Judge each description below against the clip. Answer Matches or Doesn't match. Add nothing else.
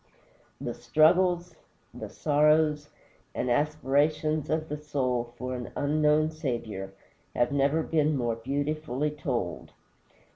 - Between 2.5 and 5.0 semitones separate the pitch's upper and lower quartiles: Matches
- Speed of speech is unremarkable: Doesn't match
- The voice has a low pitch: Doesn't match